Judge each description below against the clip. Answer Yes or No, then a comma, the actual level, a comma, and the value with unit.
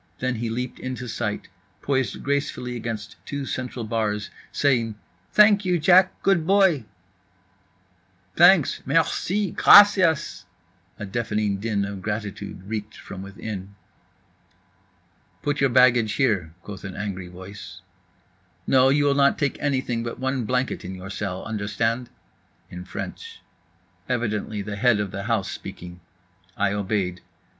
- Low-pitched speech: Yes, low, 115 Hz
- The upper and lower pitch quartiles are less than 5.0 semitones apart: No, average, 5.3 semitones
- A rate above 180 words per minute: No, slow, 135 wpm